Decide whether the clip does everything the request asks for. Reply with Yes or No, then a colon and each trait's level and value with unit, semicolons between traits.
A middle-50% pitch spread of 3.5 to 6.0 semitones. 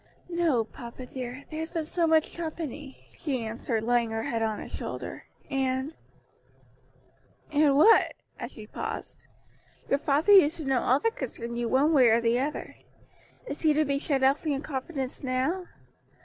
Yes: average, 4.2 semitones